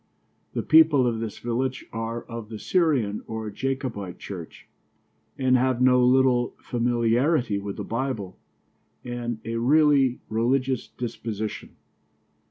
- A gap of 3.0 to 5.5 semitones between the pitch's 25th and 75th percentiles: No, narrow, 2.6 semitones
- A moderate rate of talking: No, slow, 120 wpm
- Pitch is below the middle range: Yes, low, 120 Hz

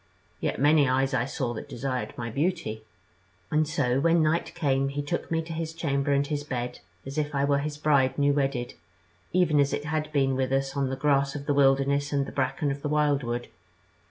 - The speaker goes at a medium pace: No, fast, 215 wpm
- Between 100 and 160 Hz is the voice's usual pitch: Yes, medium, 140 Hz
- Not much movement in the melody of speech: Yes, narrow, 1.8 semitones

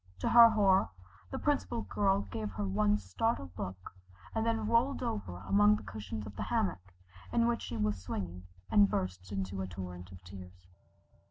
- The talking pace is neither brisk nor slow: Yes, average, 175 wpm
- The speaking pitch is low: Yes, low, 100 Hz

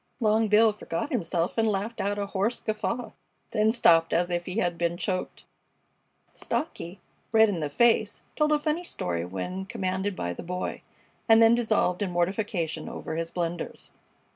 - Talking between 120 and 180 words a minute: Yes, average, 165 wpm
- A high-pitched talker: Yes, high, 195 Hz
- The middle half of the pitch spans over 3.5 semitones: Yes, average, 4.4 semitones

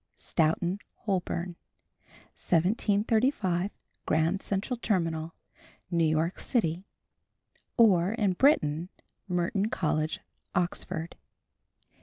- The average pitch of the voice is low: No, medium, 180 Hz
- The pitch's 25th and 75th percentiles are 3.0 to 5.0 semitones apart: Yes, average, 3.7 semitones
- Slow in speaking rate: Yes, slow, 75 wpm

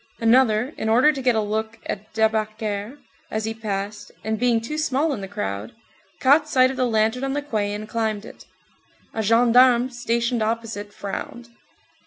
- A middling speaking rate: Yes, average, 175 wpm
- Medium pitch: No, high, 225 Hz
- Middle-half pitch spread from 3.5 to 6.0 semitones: No, average, 2.8 semitones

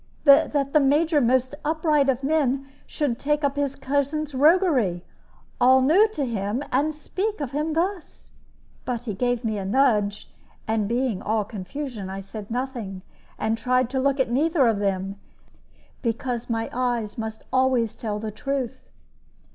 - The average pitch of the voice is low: No, very high, 255 Hz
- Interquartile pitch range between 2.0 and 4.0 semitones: No, average, 4.5 semitones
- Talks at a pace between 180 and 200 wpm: No, average, 155 wpm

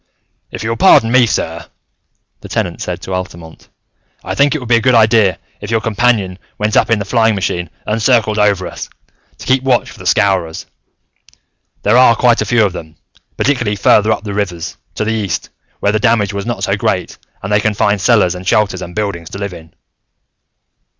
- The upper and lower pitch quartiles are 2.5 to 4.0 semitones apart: Yes, average, 3.3 semitones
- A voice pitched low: Yes, low, 105 Hz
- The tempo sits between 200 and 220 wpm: Yes, fast, 205 wpm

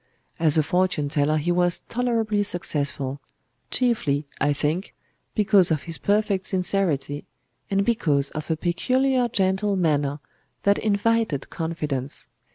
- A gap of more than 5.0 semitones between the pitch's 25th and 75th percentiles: Yes, wide, 5.6 semitones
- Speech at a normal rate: No, slow, 120 wpm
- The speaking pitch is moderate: Yes, medium, 175 Hz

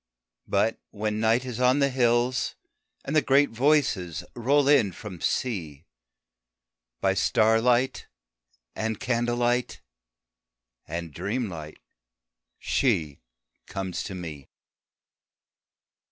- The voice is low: Yes, low, 115 Hz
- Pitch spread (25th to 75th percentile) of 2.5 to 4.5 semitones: No, average, 5.3 semitones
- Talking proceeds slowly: Yes, slow, 95 wpm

